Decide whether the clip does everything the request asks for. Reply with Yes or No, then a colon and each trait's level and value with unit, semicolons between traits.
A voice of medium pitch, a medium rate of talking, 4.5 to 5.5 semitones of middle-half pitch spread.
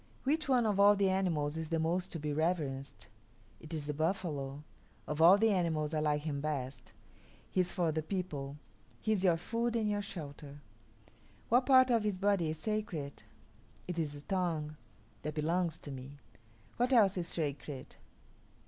Yes: medium, 165 Hz; average, 175 wpm; average, 5.0 semitones